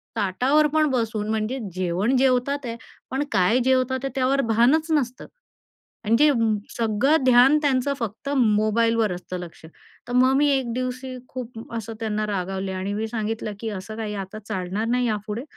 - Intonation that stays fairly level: No, average, 3.6 semitones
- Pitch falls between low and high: No, high, 230 Hz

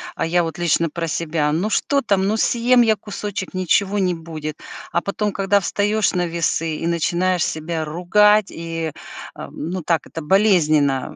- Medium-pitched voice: Yes, medium, 175 Hz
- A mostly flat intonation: No, average, 3.7 semitones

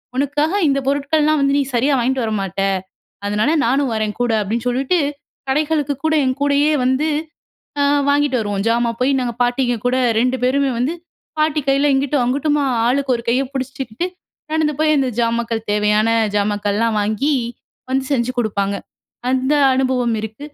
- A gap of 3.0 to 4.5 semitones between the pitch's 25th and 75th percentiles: Yes, average, 3.7 semitones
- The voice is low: No, very high, 260 Hz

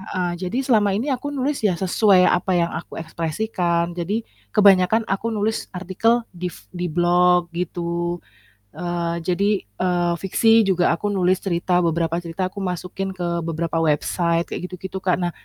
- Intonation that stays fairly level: Yes, narrow, 2.3 semitones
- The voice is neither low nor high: Yes, medium, 180 Hz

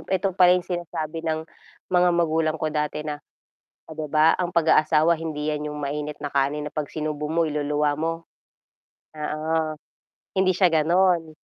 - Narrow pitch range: Yes, narrow, 1.9 semitones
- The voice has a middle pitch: Yes, medium, 155 Hz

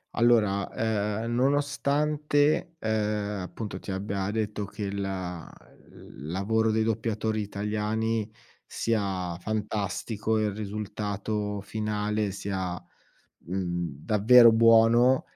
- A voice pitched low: Yes, low, 105 Hz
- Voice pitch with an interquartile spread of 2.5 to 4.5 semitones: No, narrow, 2.0 semitones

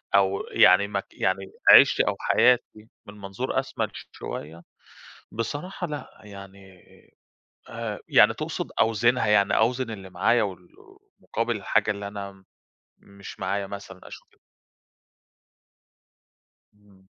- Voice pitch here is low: Yes, low, 100 Hz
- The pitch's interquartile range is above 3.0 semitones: No, narrow, 2.4 semitones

